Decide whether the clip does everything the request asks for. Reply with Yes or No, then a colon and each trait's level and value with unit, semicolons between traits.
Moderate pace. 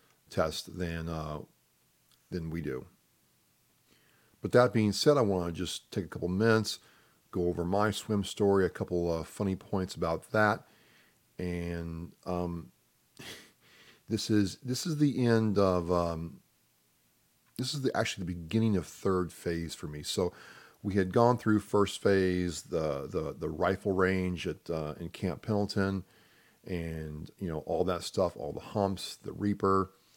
Yes: average, 155 wpm